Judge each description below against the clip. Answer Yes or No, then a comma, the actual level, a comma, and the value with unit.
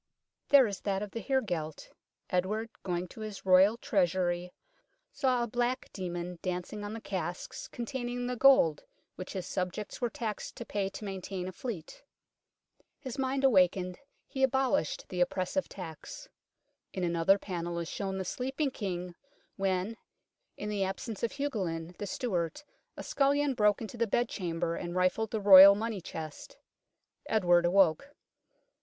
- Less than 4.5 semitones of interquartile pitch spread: No, average, 4.9 semitones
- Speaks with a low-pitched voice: No, high, 195 Hz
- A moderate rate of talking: Yes, average, 150 wpm